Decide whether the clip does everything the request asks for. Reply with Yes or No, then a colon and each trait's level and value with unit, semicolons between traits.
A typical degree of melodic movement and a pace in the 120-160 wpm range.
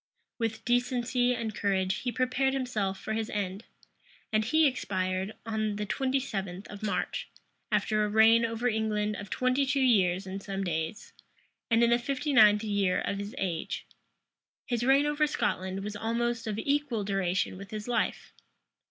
No: average, 3.8 semitones; average, 170 wpm